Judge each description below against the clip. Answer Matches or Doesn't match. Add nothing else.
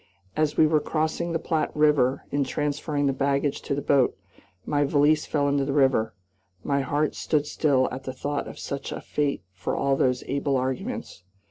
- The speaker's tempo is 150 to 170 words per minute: Doesn't match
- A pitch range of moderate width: Doesn't match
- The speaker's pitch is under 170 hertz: Matches